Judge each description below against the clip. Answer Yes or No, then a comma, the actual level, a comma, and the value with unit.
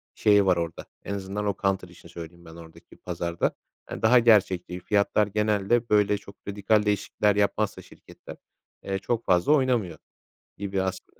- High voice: No, low, 100 Hz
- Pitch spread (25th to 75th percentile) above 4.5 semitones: No, average, 2.8 semitones